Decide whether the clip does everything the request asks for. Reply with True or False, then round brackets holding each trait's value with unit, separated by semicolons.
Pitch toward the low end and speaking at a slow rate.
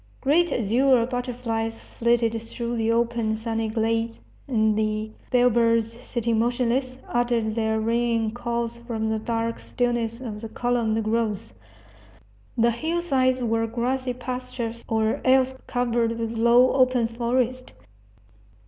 False (235 Hz; 120 wpm)